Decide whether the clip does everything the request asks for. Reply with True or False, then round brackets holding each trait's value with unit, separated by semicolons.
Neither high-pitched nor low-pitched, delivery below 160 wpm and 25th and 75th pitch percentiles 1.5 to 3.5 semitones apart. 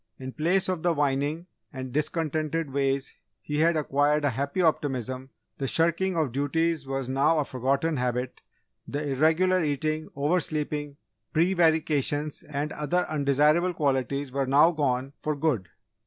True (145 Hz; 140 wpm; 2.8 semitones)